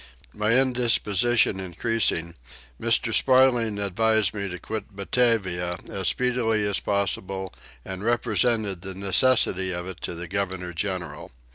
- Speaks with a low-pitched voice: Yes, low, 100 Hz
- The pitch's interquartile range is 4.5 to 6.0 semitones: No, average, 3.6 semitones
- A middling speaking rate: No, slow, 125 wpm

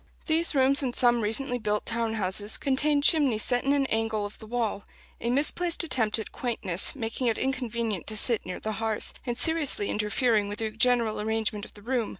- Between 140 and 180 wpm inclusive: No, average, 195 wpm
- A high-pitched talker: Yes, high, 230 Hz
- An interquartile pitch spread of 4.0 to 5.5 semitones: No, average, 3.6 semitones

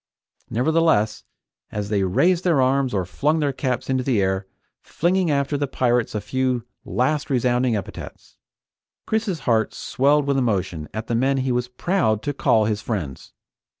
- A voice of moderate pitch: No, low, 125 Hz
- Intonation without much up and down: No, average, 4.8 semitones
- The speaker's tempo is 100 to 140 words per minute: No, average, 160 wpm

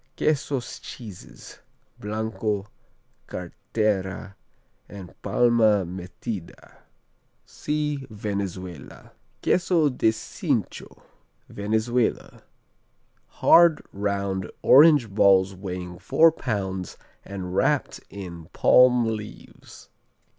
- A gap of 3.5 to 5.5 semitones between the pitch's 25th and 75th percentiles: Yes, average, 4.2 semitones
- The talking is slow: Yes, slow, 75 wpm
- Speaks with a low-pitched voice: Yes, low, 105 Hz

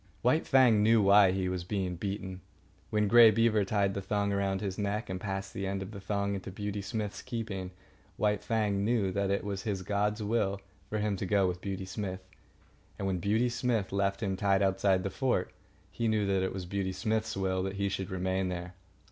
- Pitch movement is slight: Yes, narrow, 1.8 semitones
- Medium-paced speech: No, fast, 210 wpm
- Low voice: Yes, low, 100 Hz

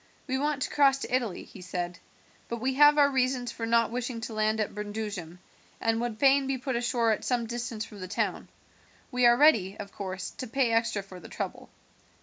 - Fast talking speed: Yes, fast, 210 wpm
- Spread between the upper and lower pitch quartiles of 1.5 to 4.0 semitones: Yes, average, 3.5 semitones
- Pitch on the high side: Yes, high, 235 Hz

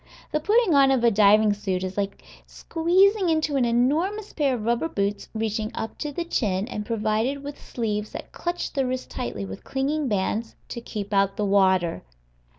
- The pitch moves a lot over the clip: Yes, wide, 6.1 semitones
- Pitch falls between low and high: No, high, 235 Hz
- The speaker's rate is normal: Yes, average, 180 wpm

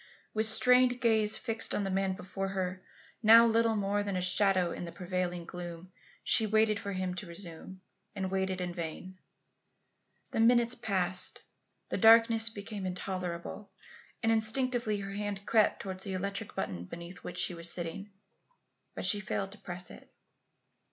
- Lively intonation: No, average, 3.2 semitones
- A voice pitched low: No, high, 195 Hz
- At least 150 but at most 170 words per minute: Yes, average, 160 wpm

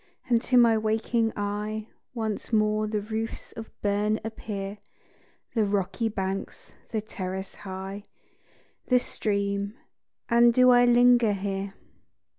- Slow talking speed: Yes, slow, 120 wpm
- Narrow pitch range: Yes, narrow, 2.2 semitones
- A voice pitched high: Yes, high, 215 Hz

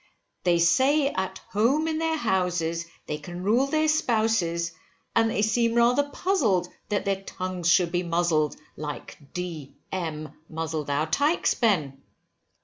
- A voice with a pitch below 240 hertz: Yes, medium, 185 Hz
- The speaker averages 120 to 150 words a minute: Yes, average, 140 wpm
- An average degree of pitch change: No, wide, 5.9 semitones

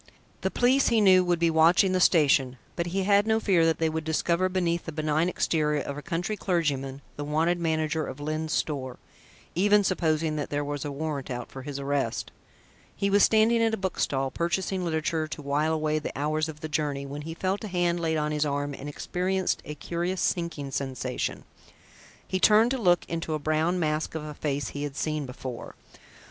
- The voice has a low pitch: No, medium, 160 Hz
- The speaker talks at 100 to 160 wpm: No, fast, 205 wpm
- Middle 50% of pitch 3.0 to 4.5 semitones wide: Yes, average, 3.5 semitones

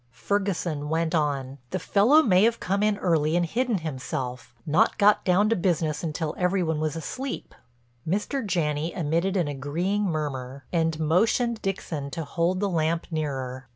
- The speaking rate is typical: Yes, average, 155 wpm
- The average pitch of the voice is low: No, medium, 165 Hz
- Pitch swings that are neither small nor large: Yes, average, 4.6 semitones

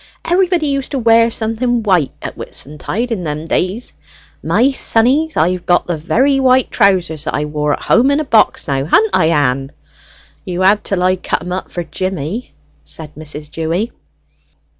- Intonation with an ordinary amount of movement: No, wide, 7.1 semitones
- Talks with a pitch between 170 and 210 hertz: Yes, medium, 185 Hz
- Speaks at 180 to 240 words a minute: No, average, 170 wpm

